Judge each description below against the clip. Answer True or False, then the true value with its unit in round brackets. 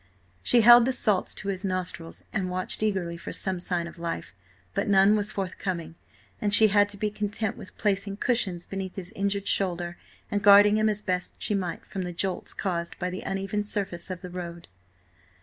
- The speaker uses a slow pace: False (195 wpm)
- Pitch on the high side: True (195 Hz)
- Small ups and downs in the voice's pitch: True (2.3 semitones)